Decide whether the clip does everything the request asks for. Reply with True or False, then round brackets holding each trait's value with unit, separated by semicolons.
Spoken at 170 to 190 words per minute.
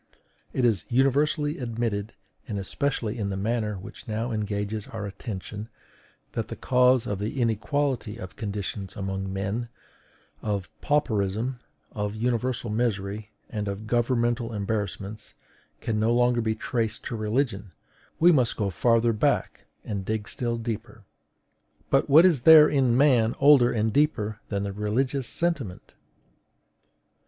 False (135 wpm)